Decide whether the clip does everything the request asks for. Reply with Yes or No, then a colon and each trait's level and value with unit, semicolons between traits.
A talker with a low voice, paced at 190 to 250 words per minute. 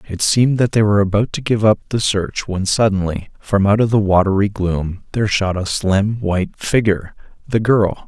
Yes: low, 105 Hz; average, 195 wpm